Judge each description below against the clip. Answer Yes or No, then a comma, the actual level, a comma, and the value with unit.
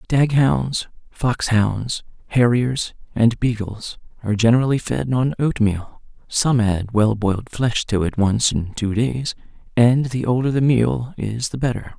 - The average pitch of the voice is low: Yes, low, 115 Hz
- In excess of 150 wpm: No, average, 145 wpm